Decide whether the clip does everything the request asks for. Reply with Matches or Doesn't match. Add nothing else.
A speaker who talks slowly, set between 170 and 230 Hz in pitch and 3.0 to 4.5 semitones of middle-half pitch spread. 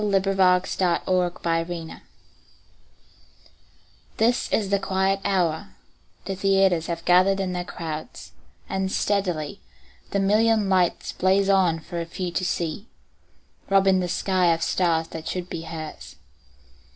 Doesn't match